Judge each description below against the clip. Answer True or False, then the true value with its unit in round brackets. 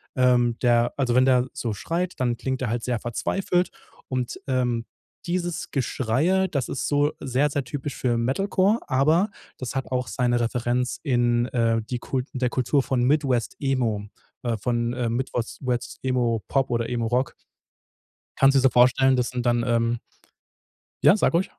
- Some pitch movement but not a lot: False (2.3 semitones)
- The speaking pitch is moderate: False (125 Hz)